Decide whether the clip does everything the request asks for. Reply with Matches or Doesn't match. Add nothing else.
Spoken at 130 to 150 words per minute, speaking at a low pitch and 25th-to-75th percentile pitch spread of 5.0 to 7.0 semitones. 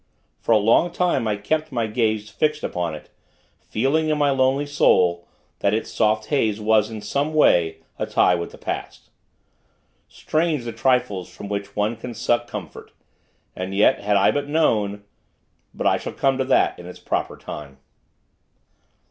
Doesn't match